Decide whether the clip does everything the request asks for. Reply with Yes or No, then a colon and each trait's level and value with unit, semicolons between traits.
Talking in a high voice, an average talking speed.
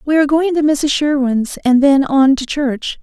No: very high, 280 Hz; fast, 220 wpm